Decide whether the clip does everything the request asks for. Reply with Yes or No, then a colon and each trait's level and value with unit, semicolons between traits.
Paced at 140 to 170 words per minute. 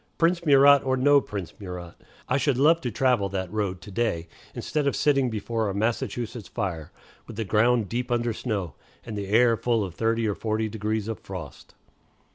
No: average, 190 wpm